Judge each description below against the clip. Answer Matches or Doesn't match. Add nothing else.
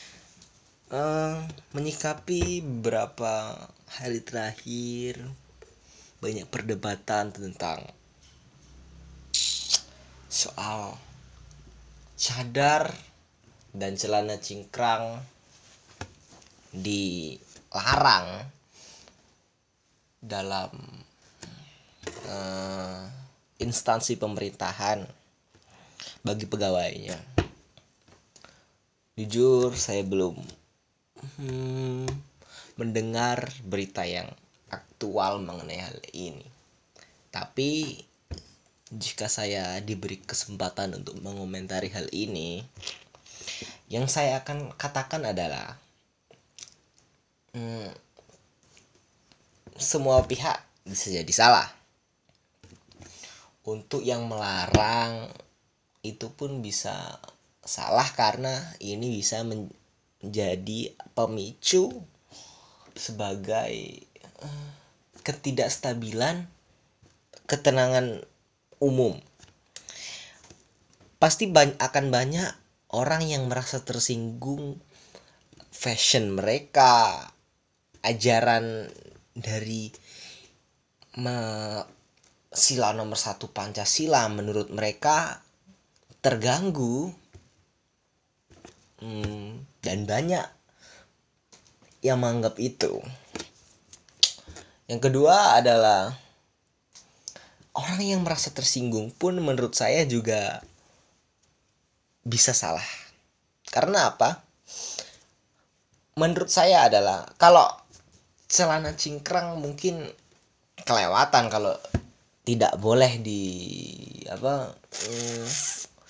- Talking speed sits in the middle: Doesn't match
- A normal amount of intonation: Matches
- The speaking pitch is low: Matches